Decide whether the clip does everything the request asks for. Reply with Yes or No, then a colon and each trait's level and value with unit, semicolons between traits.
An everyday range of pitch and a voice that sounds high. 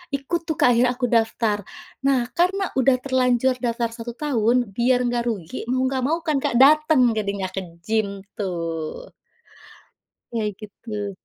Yes: average, 3.8 semitones; high, 240 Hz